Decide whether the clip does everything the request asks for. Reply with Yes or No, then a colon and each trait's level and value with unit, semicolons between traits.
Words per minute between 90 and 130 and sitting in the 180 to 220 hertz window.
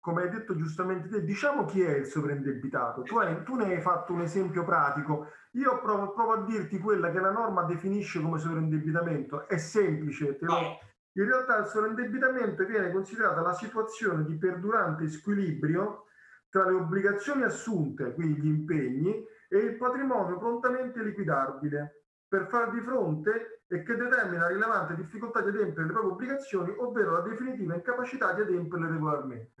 No: average, 160 wpm; high, 190 Hz